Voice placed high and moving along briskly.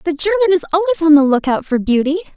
Yes: very high, 325 Hz; fast, 230 wpm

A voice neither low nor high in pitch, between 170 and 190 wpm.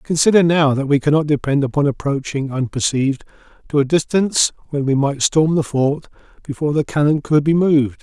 Yes: medium, 145 Hz; average, 180 wpm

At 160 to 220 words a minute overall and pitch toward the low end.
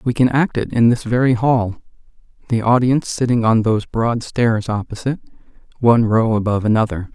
Yes: average, 170 wpm; low, 115 Hz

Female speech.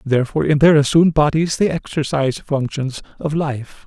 No: male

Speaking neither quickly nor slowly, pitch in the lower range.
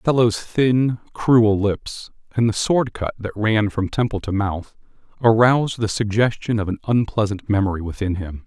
Yes: average, 170 wpm; low, 110 Hz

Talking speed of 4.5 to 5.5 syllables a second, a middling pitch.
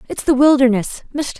No: 5.4 syllables/s; very high, 265 Hz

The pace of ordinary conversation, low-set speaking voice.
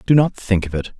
No: fast, 305 wpm; low, 110 Hz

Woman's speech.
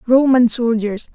Yes: female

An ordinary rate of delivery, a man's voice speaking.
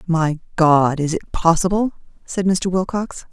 No: average, 145 wpm; female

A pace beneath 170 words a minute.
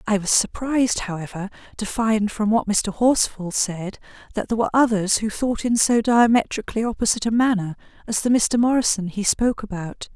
No: average, 175 wpm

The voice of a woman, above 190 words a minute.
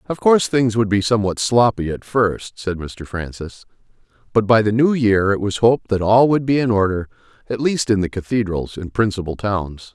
No: male; fast, 205 wpm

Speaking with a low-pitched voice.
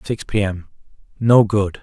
Yes: low, 105 Hz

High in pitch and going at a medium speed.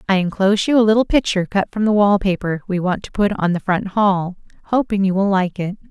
No: high, 195 Hz; fast, 245 wpm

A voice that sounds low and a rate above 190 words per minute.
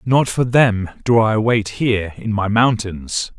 No: low, 110 Hz; average, 175 wpm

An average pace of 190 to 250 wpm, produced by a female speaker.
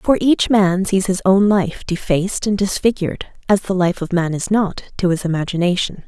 Yes: average, 200 wpm; female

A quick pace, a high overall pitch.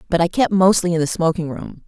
No: fast, 255 wpm; medium, 170 Hz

